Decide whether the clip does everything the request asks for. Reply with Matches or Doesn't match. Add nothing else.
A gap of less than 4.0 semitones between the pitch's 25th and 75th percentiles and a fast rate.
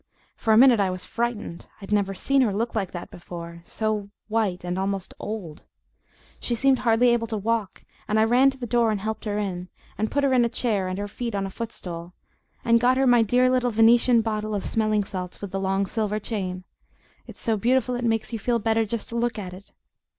Matches